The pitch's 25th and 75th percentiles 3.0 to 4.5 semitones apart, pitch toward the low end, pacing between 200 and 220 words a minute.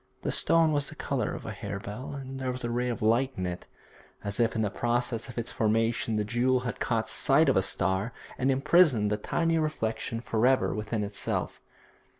Yes: average, 3.5 semitones; low, 120 Hz; fast, 205 wpm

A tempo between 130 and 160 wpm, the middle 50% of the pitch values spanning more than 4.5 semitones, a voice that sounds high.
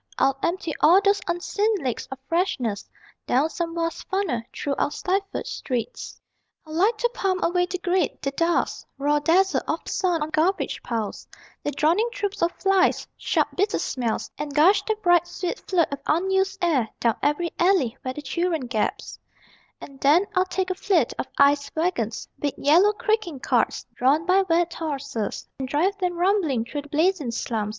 No: average, 175 wpm; average, 5.1 semitones; very high, 335 Hz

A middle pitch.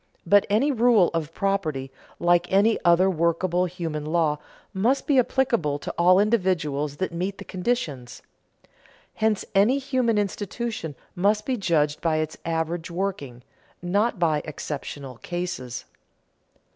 Yes: medium, 180 Hz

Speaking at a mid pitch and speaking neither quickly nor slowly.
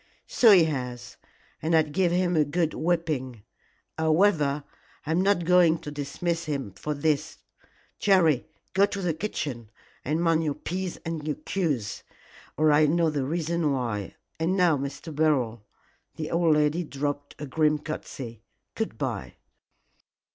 Yes: medium, 155 Hz; average, 145 wpm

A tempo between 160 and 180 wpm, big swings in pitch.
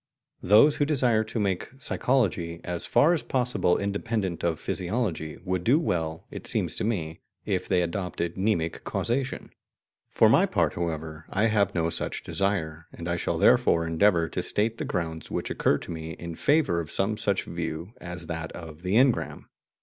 No: average, 175 wpm; average, 4.8 semitones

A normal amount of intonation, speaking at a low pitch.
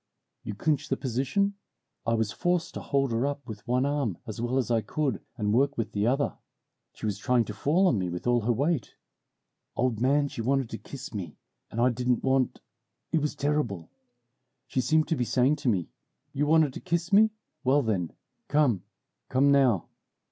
Yes: average, 4.2 semitones; low, 130 Hz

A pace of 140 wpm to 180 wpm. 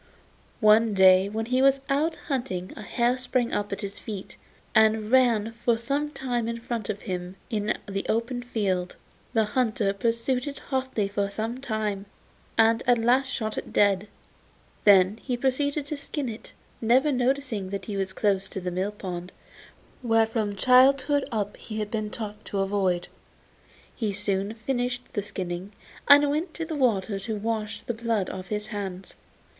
Yes: average, 170 wpm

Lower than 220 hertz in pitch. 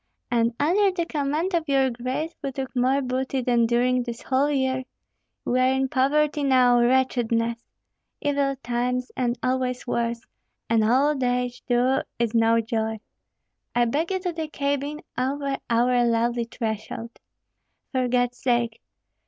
No: very high, 255 Hz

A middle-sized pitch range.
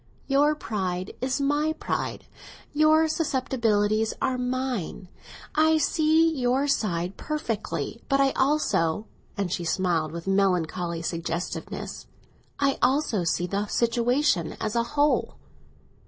No: wide, 7.5 semitones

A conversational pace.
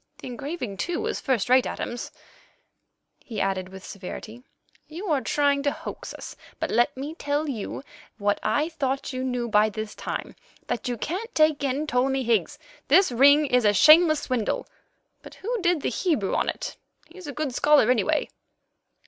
Yes: average, 170 wpm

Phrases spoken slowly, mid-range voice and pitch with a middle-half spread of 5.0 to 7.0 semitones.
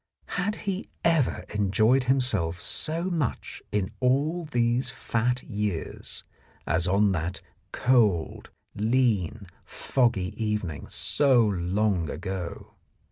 No: slow, 100 wpm; low, 110 Hz; wide, 5.6 semitones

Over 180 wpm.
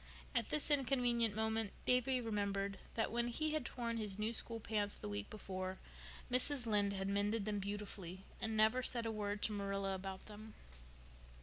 No: average, 175 wpm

